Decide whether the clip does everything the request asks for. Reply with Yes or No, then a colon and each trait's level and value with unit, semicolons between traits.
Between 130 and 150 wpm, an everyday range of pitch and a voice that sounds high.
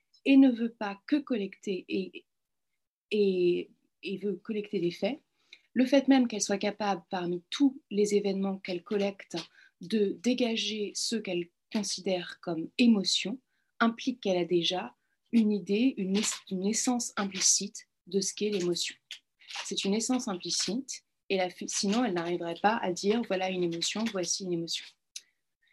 Yes: slow, 145 wpm; average, 3.7 semitones; high, 200 Hz